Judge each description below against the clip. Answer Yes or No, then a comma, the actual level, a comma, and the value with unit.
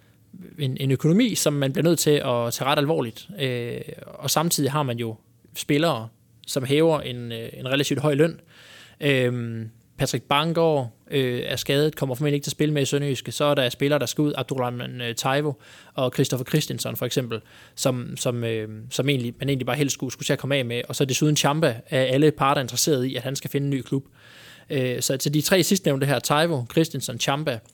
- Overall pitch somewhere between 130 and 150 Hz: Yes, medium, 140 Hz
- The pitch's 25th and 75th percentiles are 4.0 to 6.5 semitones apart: No, average, 3.2 semitones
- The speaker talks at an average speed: Yes, average, 215 wpm